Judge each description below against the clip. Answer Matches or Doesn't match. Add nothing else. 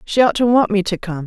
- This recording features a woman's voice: Matches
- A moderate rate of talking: Doesn't match